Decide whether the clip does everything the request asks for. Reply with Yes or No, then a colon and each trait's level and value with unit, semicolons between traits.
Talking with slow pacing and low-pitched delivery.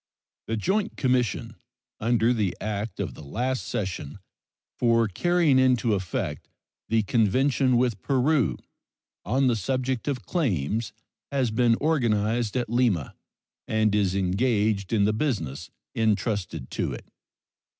Yes: slow, 125 wpm; low, 115 Hz